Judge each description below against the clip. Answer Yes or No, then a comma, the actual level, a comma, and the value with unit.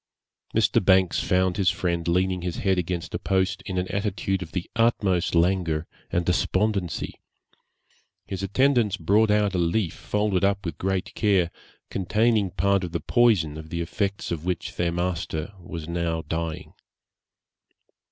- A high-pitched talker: No, very low, 90 Hz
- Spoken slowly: No, average, 150 wpm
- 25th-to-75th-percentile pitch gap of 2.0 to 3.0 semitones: Yes, narrow, 2.6 semitones